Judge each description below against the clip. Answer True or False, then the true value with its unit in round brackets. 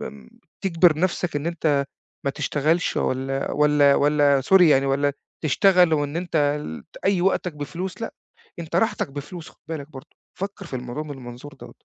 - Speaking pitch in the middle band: True (150 Hz)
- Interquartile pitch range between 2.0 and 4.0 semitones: True (3.7 semitones)